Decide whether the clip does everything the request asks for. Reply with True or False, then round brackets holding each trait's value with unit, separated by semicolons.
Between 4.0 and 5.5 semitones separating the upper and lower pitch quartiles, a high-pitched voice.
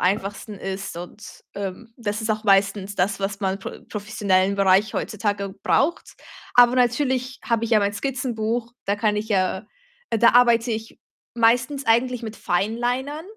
False (3.3 semitones; 215 Hz)